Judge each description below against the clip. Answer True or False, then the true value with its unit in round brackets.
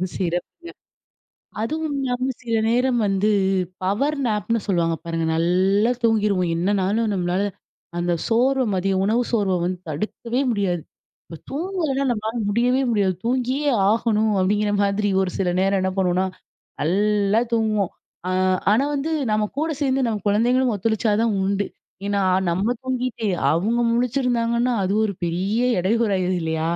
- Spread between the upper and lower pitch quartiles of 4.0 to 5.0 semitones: True (4.3 semitones)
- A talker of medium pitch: False (210 Hz)